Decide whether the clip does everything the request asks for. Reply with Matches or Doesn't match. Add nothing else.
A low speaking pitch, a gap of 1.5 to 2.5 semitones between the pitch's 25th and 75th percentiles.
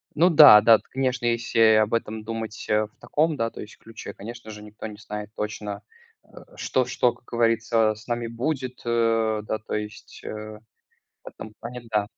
Matches